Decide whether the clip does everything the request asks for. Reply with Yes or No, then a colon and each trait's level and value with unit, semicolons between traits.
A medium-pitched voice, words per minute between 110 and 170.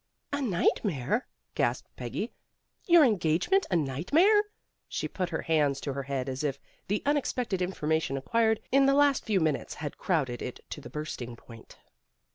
Yes: medium, 170 Hz; average, 165 wpm